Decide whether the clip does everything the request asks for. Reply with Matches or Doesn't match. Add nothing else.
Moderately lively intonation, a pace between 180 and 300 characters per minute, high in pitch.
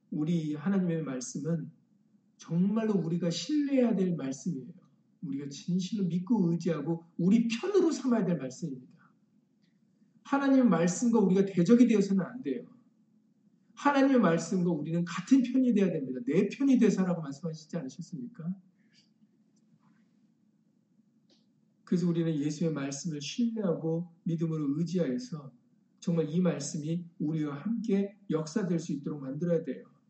Doesn't match